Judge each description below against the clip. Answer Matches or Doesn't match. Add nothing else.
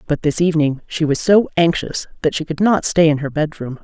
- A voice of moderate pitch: Matches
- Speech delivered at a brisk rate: Matches